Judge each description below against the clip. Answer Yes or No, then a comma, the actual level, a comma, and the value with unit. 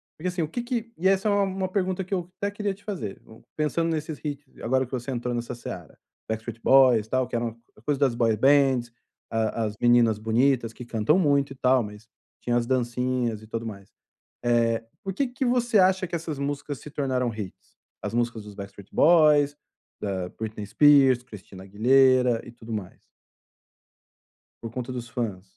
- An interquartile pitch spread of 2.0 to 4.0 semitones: No, average, 5.2 semitones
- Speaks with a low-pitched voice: Yes, low, 125 Hz